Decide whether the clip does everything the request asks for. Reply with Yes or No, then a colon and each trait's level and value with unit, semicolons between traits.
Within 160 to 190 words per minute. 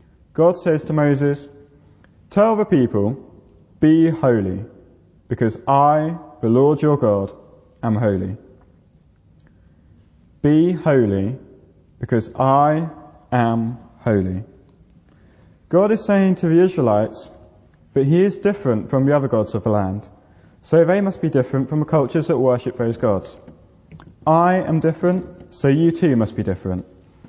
No: slow, 135 wpm